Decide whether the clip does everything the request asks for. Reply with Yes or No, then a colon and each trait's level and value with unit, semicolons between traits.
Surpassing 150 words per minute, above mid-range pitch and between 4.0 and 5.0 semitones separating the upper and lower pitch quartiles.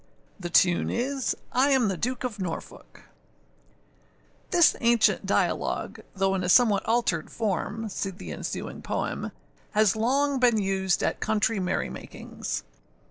No: slow, 135 wpm; high, 220 Hz; average, 4.4 semitones